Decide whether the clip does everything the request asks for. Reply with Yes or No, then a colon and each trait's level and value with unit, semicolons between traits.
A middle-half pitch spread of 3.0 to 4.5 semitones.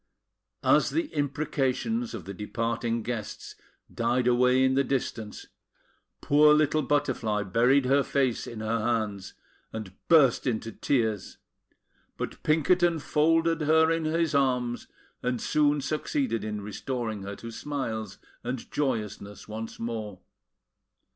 No: average, 4.9 semitones